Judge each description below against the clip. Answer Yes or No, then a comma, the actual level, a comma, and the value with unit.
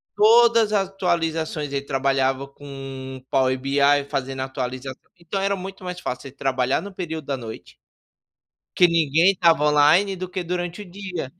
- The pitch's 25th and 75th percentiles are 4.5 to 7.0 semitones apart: Yes, wide, 5.4 semitones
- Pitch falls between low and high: Yes, medium, 155 Hz